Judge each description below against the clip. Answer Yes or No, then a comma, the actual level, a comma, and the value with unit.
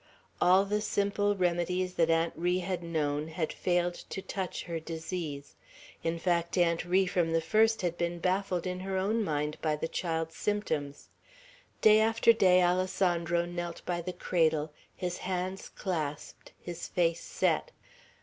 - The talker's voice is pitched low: No, medium, 175 Hz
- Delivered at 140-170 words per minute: Yes, average, 155 wpm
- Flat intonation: Yes, narrow, 2.3 semitones